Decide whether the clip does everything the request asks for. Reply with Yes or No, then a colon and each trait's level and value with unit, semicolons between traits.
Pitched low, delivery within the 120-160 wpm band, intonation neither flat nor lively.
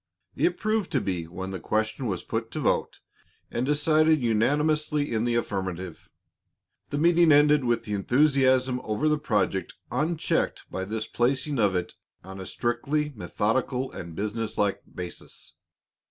No: low, 120 Hz; average, 145 wpm; wide, 6.4 semitones